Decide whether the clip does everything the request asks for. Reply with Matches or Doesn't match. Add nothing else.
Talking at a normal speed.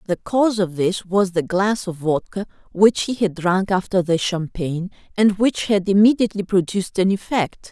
Matches